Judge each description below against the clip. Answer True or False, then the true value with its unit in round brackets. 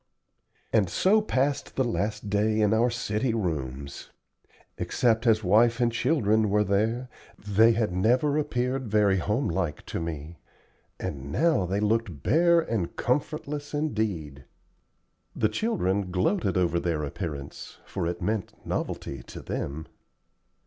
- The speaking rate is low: True (130 wpm)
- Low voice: True (105 Hz)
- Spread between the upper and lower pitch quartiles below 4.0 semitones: False (5.4 semitones)